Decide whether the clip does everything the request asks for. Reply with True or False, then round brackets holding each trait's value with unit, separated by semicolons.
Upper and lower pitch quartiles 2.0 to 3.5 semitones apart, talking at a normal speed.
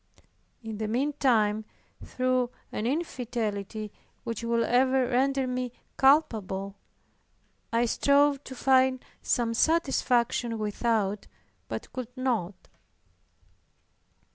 False (3.2 semitones; 90 wpm)